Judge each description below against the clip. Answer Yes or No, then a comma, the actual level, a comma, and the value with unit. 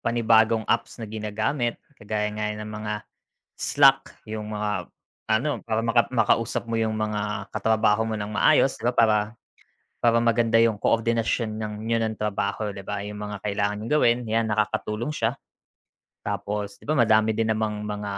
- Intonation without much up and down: Yes, narrow, 1.5 semitones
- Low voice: Yes, low, 110 Hz